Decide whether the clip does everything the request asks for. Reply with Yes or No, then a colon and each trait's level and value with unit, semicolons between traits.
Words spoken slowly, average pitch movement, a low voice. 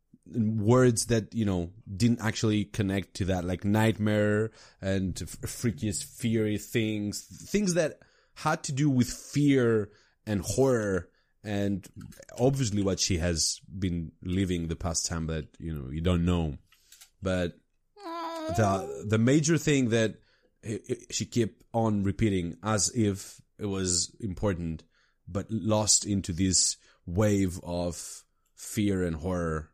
Yes: slow, 130 wpm; average, 4.0 semitones; low, 105 Hz